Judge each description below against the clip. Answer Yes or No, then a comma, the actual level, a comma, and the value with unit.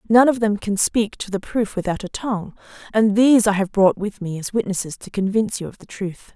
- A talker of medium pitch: No, high, 205 Hz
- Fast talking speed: Yes, fast, 245 wpm